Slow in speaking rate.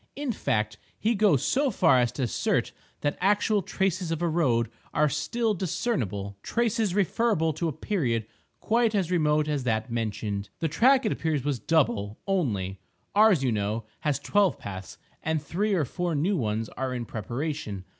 No: average, 165 wpm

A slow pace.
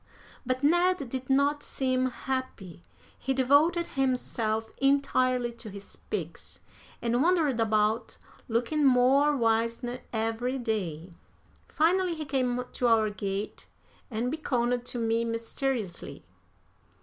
Yes: slow, 115 wpm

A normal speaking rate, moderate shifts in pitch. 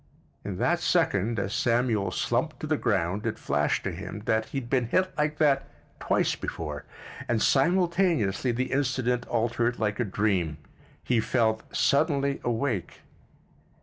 Yes: average, 145 wpm; average, 4.7 semitones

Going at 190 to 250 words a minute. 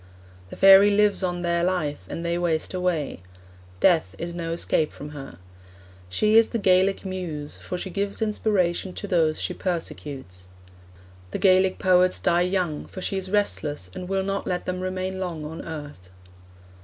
No: average, 170 wpm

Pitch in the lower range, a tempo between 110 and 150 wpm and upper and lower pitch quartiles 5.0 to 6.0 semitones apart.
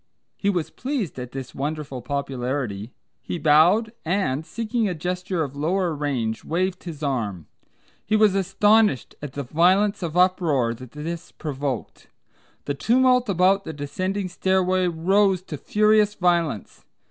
No: medium, 170 Hz; average, 140 wpm; wide, 5.5 semitones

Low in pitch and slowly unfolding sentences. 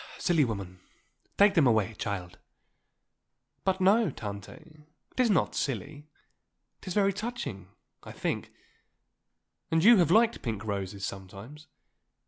No: medium, 150 Hz; slow, 125 wpm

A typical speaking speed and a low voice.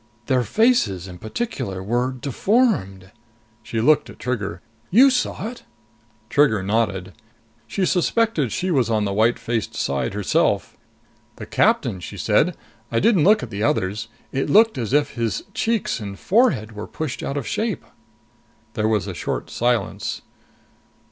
Yes: average, 150 wpm; low, 120 Hz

